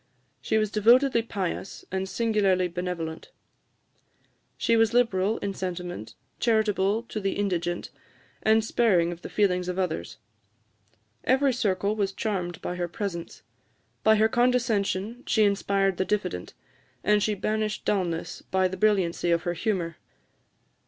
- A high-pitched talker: Yes, high, 200 Hz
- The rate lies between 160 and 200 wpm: No, slow, 135 wpm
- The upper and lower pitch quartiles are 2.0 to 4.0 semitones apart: Yes, average, 3.3 semitones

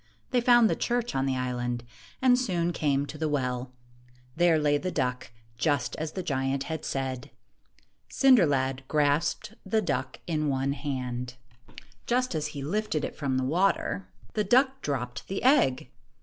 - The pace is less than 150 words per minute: No, average, 170 wpm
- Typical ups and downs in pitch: No, wide, 6.6 semitones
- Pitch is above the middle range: No, medium, 150 Hz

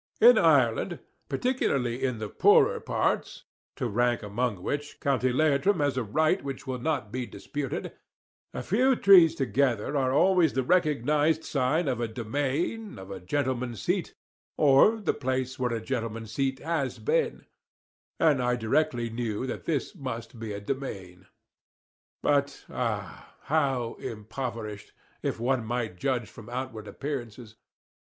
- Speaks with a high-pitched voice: No, low, 130 Hz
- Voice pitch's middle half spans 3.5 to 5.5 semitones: Yes, average, 4.1 semitones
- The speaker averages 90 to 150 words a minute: Yes, average, 145 wpm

